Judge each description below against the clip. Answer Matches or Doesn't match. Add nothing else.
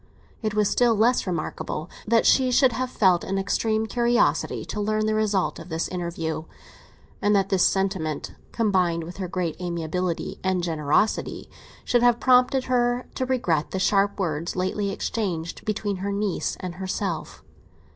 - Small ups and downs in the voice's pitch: Doesn't match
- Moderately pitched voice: Doesn't match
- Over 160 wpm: Doesn't match